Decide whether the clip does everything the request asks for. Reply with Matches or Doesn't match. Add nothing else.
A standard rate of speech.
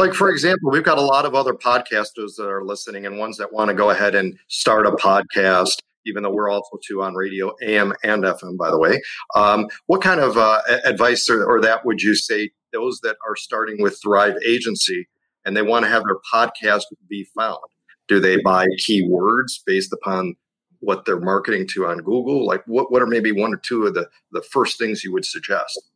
Doesn't match